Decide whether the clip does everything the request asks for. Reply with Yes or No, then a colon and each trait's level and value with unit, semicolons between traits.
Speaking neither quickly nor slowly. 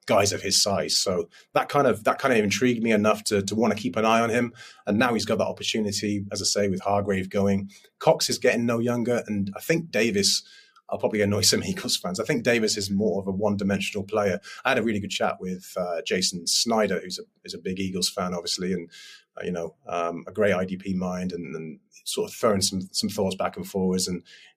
No: fast, 240 wpm